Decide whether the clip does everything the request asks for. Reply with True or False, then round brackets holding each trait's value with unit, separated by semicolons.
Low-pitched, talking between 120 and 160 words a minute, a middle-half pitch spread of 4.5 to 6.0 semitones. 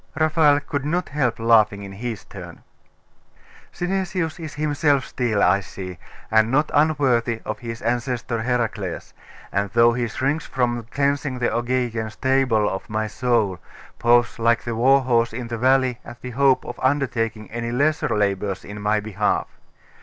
False (120 Hz; 155 wpm; 3.7 semitones)